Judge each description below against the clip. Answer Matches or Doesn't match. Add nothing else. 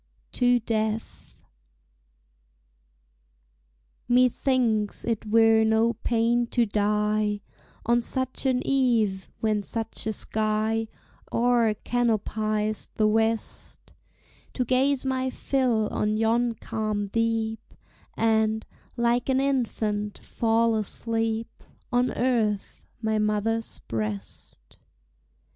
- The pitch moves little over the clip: Matches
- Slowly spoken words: Matches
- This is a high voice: Matches